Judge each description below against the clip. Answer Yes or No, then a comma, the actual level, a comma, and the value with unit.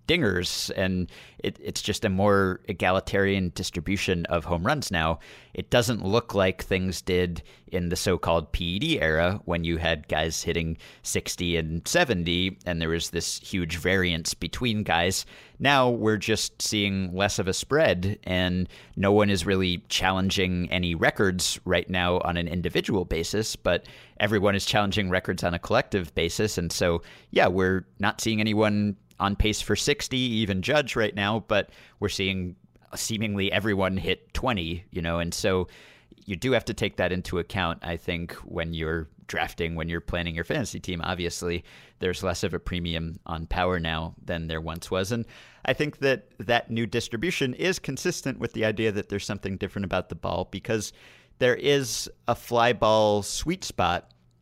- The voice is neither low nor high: No, very low, 95 Hz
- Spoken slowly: No, average, 175 wpm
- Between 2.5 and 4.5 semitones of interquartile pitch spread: Yes, average, 3.6 semitones